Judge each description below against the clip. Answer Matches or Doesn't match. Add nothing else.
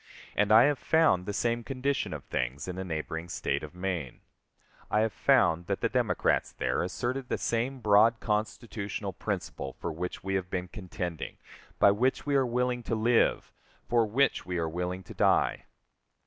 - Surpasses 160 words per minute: Matches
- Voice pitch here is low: Matches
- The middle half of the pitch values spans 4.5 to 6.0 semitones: Matches